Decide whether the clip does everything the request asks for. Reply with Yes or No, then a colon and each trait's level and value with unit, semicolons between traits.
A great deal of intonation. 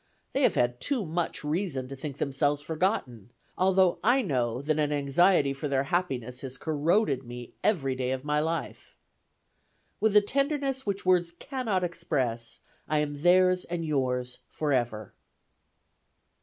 Yes: wide, 5.7 semitones